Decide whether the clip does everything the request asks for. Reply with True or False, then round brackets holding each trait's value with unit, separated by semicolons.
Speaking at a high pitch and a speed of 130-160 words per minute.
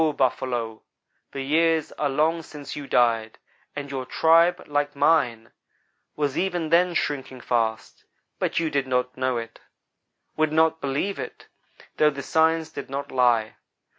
False (140 Hz; 145 wpm)